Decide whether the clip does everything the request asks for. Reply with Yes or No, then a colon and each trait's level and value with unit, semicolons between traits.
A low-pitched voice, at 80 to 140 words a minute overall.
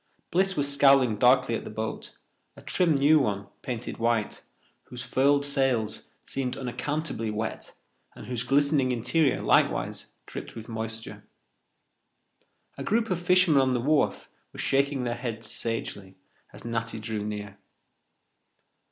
Yes: low, 125 Hz; slow, 135 wpm